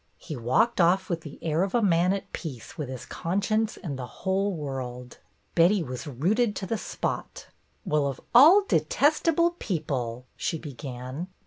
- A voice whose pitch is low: No, medium, 165 Hz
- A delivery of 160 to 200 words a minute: Yes, average, 165 wpm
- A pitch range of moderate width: No, wide, 7.1 semitones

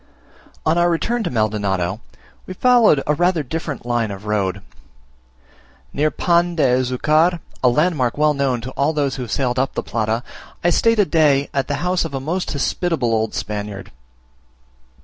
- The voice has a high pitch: No, medium, 140 Hz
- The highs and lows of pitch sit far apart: Yes, wide, 6.1 semitones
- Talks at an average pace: Yes, average, 170 wpm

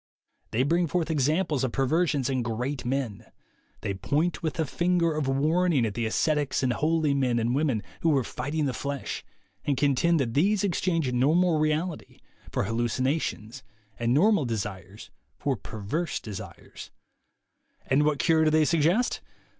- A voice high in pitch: No, medium, 145 Hz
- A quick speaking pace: No, average, 155 wpm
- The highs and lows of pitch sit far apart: No, average, 4.7 semitones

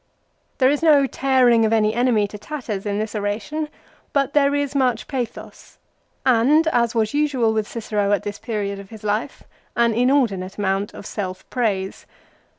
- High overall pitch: Yes, high, 230 Hz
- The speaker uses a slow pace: No, average, 165 wpm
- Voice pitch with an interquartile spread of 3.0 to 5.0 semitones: Yes, average, 4.5 semitones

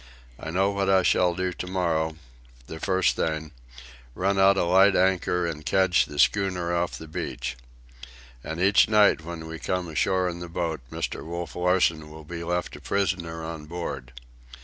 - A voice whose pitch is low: Yes, very low, 85 Hz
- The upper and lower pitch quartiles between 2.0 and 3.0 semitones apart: Yes, average, 2.7 semitones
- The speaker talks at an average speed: Yes, average, 170 wpm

